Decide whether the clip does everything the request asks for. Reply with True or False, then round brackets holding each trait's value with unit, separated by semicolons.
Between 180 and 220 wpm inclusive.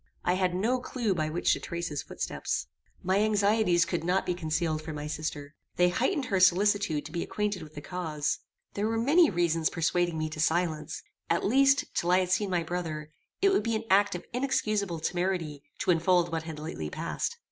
True (200 wpm)